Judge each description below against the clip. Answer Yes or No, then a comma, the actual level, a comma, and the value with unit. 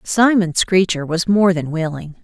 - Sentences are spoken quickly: No, average, 160 wpm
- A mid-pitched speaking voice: Yes, medium, 180 Hz